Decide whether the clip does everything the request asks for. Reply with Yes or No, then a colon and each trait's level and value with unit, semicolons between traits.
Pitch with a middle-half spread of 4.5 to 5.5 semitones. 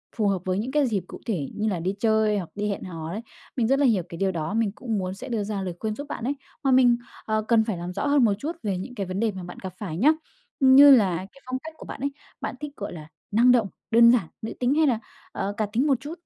Yes: average, 5.0 semitones